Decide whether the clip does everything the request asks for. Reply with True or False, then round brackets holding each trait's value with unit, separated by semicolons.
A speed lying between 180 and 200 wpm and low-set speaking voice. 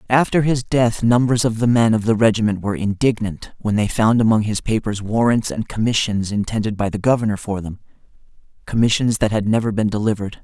True (190 wpm; 110 Hz)